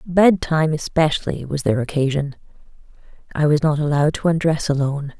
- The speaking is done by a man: No, female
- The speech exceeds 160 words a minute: No, average, 150 wpm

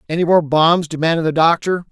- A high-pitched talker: No, medium, 165 Hz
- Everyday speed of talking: Yes, average, 190 wpm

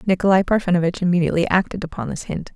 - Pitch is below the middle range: No, medium, 180 Hz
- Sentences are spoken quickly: No, average, 165 wpm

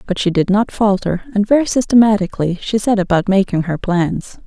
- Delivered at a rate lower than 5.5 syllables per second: No, 5.6 syllables/s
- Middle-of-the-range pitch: No, high, 200 Hz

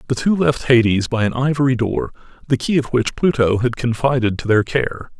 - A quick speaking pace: Yes, fast, 210 wpm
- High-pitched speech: No, low, 125 Hz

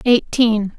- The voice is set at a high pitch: Yes, high, 225 Hz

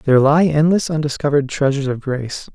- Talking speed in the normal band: Yes, average, 165 wpm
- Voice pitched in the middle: Yes, medium, 145 Hz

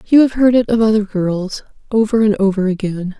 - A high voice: Yes, high, 210 Hz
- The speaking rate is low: No, fast, 205 wpm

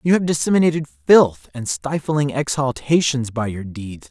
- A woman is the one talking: No, male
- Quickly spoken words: No, average, 145 wpm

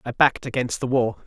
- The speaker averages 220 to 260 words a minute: Yes, fast, 235 wpm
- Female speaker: No, male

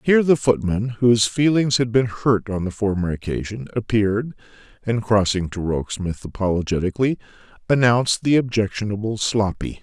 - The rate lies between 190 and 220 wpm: No, slow, 135 wpm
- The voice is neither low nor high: No, low, 110 Hz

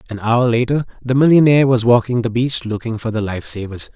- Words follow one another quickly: Yes, fast, 210 wpm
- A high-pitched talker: No, low, 120 Hz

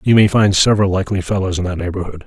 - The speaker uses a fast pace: Yes, fast, 240 wpm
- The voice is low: Yes, very low, 95 Hz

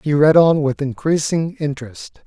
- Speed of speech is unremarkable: Yes, average, 160 wpm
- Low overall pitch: No, medium, 150 Hz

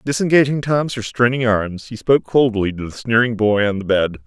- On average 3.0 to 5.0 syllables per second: No, 5.4 syllables/s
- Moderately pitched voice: No, low, 115 Hz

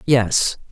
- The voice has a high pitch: No, low, 120 Hz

